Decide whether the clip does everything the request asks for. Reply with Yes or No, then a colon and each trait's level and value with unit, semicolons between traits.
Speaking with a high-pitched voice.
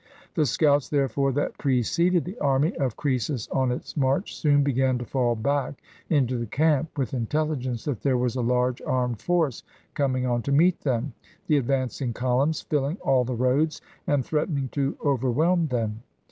No: low, 135 Hz